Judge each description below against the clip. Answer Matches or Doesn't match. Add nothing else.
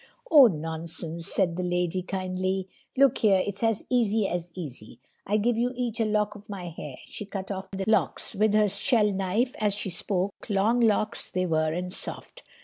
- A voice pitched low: Doesn't match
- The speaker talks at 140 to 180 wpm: Doesn't match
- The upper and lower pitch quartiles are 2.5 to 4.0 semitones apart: Matches